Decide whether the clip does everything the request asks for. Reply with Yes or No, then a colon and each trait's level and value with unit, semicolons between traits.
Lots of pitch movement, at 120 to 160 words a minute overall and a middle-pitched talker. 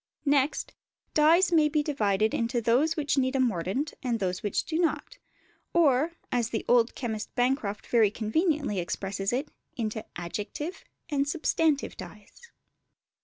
No: wide, 5.9 semitones; average, 140 wpm; very high, 255 Hz